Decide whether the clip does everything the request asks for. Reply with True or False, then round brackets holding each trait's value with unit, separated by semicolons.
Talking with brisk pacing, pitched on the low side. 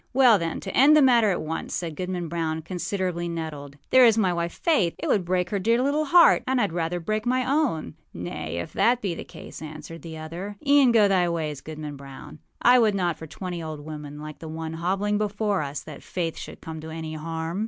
False (225 wpm; 170 Hz)